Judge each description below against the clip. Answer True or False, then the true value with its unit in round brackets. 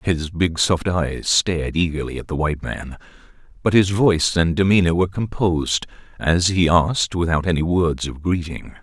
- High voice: False (85 Hz)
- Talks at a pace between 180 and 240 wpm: False (170 wpm)